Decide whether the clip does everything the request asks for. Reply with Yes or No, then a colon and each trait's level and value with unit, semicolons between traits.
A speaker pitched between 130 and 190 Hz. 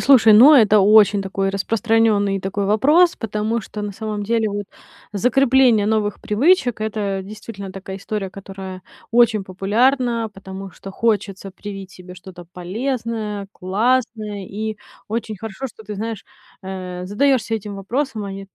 No: high, 210 Hz